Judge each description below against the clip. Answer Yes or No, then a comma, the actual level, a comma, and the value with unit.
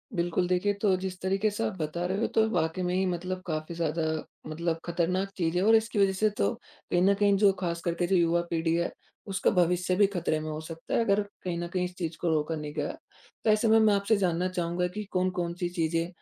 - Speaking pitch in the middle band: Yes, medium, 180 Hz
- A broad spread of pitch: No, narrow, 2.5 semitones